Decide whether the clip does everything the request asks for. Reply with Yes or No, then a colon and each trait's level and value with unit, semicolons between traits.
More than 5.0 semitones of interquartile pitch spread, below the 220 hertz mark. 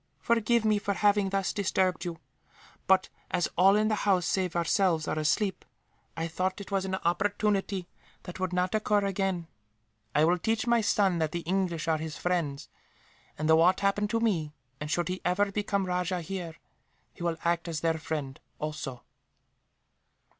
No: average, 3.2 semitones; medium, 185 Hz